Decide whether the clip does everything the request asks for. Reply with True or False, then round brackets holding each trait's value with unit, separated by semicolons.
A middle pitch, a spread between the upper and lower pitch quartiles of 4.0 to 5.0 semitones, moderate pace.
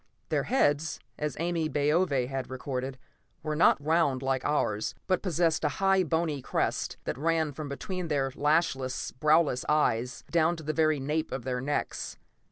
False (150 Hz; 3.5 semitones; 165 wpm)